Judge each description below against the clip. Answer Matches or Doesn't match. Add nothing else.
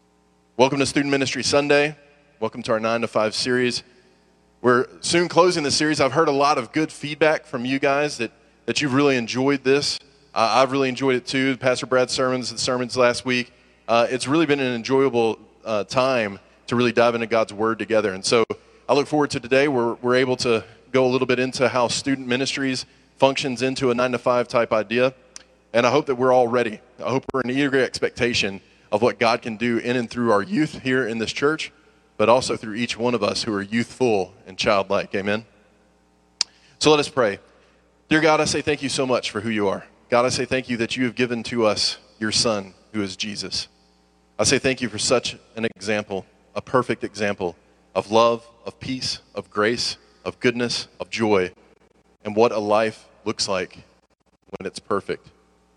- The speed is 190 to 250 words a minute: Matches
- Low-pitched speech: Matches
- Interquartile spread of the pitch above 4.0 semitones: Doesn't match